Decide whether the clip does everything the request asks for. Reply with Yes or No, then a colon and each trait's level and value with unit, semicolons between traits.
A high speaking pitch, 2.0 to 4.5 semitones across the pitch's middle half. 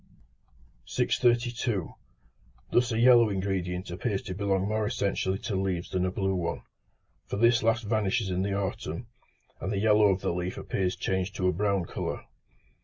No: low, 100 Hz; average, 2.8 semitones